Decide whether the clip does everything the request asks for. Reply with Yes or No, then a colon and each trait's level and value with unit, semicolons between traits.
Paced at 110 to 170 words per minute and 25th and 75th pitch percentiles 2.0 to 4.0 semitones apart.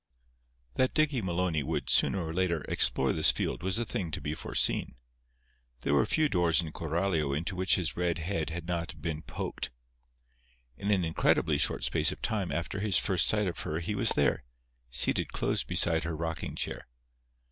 No: average, 180 wpm; average, 2.8 semitones